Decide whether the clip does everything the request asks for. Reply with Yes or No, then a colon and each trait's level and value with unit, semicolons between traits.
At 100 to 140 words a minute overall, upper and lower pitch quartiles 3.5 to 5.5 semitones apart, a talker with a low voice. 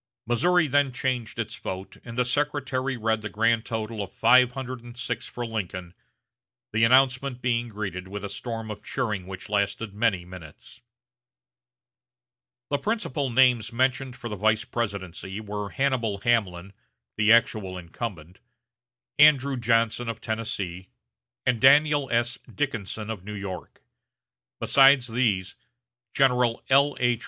Yes: slow, 135 wpm; average, 3.9 semitones; low, 115 Hz